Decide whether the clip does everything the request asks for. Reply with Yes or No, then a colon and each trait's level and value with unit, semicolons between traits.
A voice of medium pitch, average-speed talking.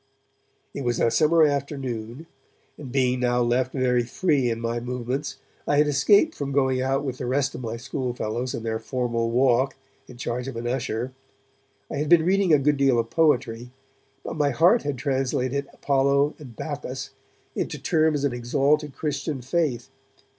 No: low, 130 Hz; average, 170 wpm